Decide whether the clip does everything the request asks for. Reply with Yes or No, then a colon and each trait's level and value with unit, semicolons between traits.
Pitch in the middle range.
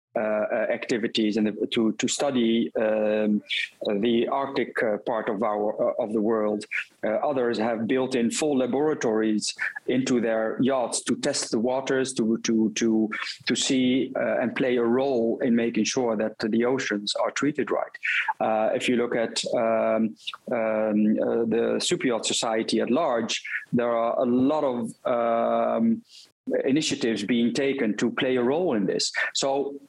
No: low, 115 Hz